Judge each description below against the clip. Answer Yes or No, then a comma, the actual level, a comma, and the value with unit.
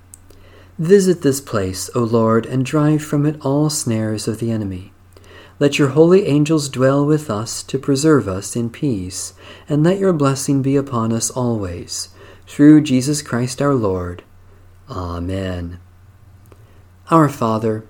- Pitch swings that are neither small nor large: No, wide, 7.0 semitones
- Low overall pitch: Yes, low, 115 Hz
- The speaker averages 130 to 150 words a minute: Yes, average, 140 wpm